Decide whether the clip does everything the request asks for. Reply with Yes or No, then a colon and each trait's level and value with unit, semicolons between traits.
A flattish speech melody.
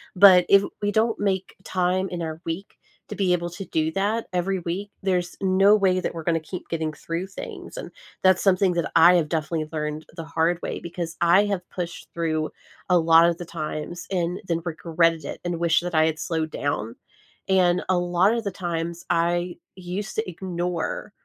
Yes: narrow, 2.2 semitones